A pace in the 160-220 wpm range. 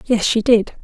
Yes: fast, 215 wpm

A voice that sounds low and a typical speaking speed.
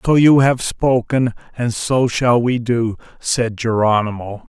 Yes: low, 120 Hz; average, 145 wpm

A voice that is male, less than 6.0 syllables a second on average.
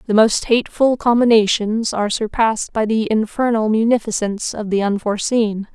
No: female; 5.4 syllables/s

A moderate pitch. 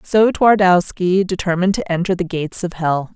Yes: medium, 180 Hz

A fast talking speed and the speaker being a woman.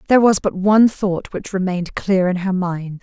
Yes: fast, 220 wpm; female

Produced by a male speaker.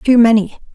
No: female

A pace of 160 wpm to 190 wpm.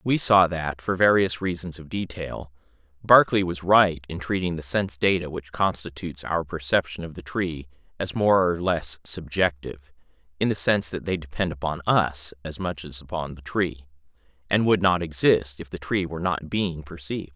Yes: average, 185 wpm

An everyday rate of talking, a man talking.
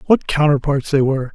Yes: average, 180 wpm; male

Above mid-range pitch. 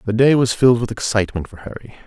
No: low, 115 Hz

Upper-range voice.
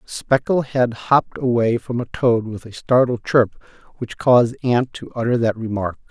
No: low, 120 Hz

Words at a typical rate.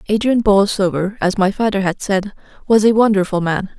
Yes: average, 175 wpm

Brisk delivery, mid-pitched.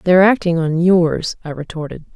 No: average, 165 wpm; medium, 170 Hz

